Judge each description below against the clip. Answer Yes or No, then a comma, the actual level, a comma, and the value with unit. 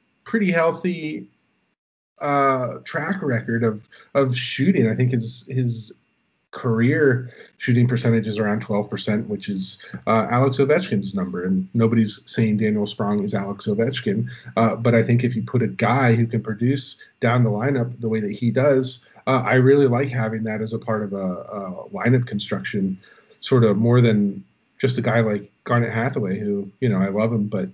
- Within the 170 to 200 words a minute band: Yes, average, 180 wpm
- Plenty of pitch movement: No, average, 3.4 semitones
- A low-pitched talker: Yes, low, 115 Hz